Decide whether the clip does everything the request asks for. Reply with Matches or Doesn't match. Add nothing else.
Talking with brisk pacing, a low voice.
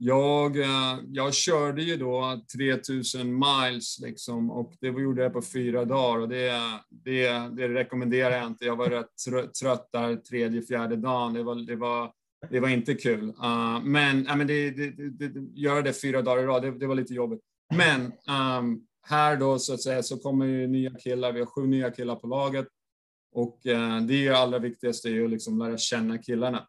Matches